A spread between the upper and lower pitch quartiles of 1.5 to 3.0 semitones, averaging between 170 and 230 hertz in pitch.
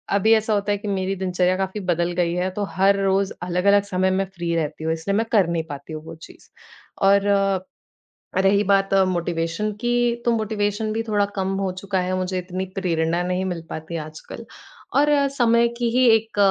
Yes: average, 2.7 semitones; high, 190 Hz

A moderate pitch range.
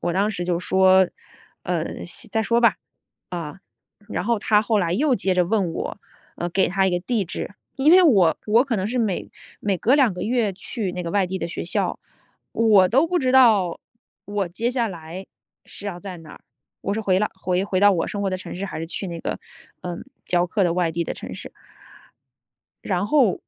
Yes: average, 3.7 semitones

